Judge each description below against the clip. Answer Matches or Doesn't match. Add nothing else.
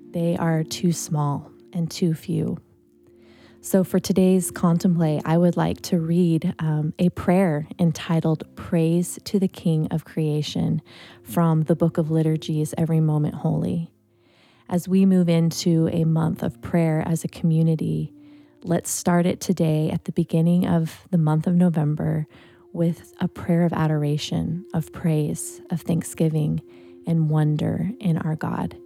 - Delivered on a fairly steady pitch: Matches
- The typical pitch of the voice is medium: Matches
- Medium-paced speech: Matches